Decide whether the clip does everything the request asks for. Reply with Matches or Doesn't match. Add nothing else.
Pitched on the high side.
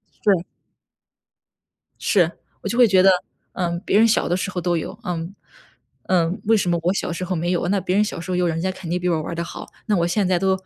Doesn't match